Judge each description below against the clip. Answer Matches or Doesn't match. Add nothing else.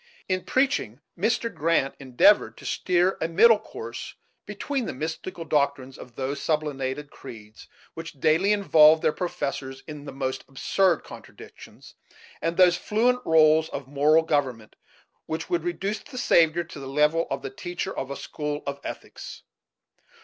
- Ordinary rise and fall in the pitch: Matches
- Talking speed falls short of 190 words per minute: Matches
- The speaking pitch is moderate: Matches